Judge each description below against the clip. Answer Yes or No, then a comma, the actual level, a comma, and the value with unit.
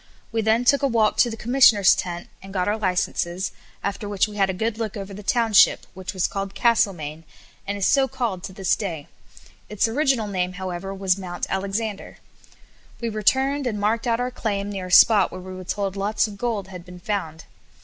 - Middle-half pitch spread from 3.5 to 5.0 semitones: No, average, 3.1 semitones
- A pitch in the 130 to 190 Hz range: No, high, 200 Hz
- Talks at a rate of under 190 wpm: No, fast, 205 wpm